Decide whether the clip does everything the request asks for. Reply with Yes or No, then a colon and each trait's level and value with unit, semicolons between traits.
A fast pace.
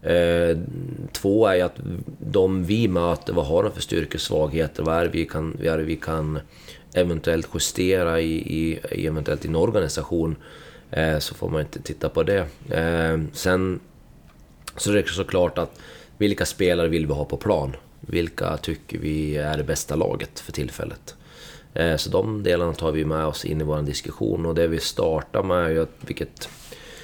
No: average, 180 wpm